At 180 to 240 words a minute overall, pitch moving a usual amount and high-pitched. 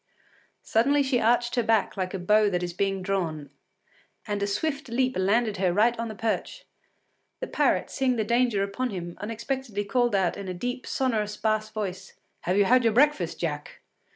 Yes: average, 185 wpm; average, 3.9 semitones; high, 215 Hz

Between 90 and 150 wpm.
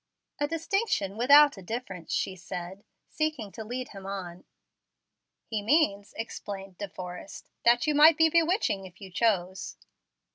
Yes: average, 145 wpm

